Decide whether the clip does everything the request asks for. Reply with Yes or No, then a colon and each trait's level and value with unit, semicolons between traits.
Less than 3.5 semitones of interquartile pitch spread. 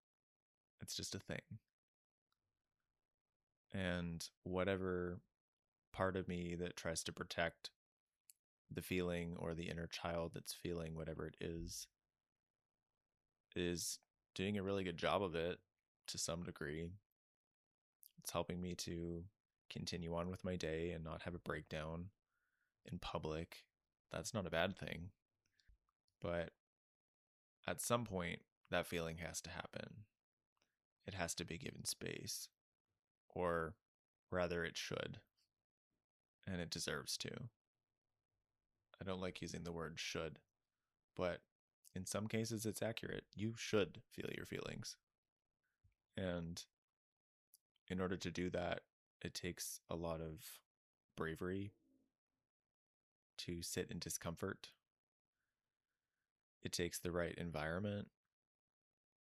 Yes: narrow, 2.5 semitones